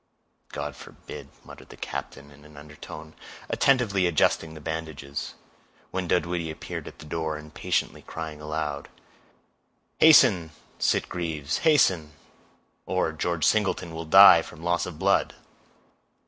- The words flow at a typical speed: No, slow, 120 wpm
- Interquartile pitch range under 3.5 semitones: Yes, narrow, 2.5 semitones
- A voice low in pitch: Yes, very low, 80 Hz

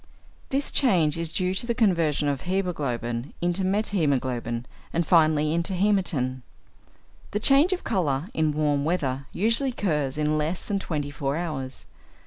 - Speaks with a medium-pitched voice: Yes, medium, 160 Hz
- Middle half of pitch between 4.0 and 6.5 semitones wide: Yes, average, 5.1 semitones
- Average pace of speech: Yes, average, 145 wpm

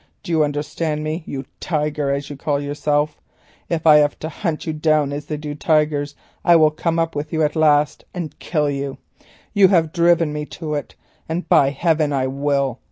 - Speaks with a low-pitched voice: No, medium, 150 Hz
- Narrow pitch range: Yes, narrow, 1.7 semitones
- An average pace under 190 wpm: No, average, 200 wpm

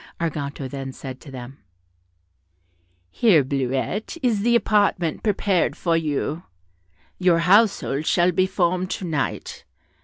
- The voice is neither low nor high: Yes, medium, 170 Hz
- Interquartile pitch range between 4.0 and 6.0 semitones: Yes, wide, 5.5 semitones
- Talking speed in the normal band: No, slow, 120 wpm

